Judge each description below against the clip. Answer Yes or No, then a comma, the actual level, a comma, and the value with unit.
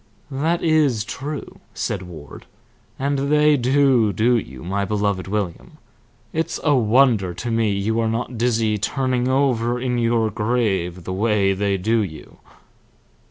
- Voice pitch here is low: Yes, low, 115 Hz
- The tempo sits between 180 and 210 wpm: No, average, 145 wpm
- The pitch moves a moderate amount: Yes, average, 4.5 semitones